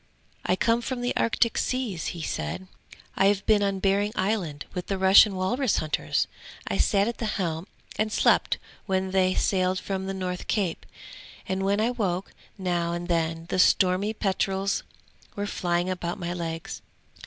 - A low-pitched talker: No, high, 190 Hz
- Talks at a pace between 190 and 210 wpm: No, average, 165 wpm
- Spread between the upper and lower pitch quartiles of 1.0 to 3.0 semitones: Yes, narrow, 2.4 semitones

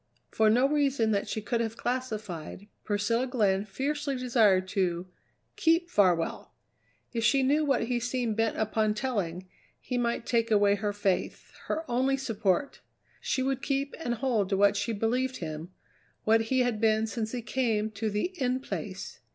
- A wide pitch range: No, average, 4.0 semitones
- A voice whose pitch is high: Yes, high, 225 Hz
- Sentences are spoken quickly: No, average, 170 wpm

